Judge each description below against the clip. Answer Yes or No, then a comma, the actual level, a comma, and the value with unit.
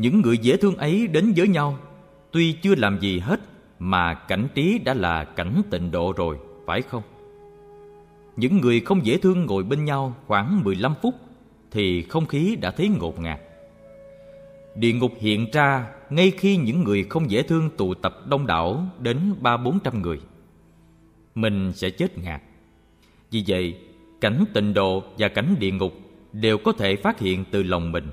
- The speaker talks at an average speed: Yes, average, 175 wpm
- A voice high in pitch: No, low, 115 Hz